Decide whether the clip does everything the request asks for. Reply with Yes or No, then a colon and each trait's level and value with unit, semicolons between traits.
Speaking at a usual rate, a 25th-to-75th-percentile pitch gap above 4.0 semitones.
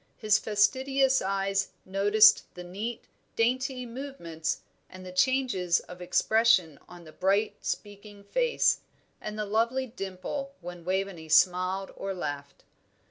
No: slow, 125 wpm; average, 4.4 semitones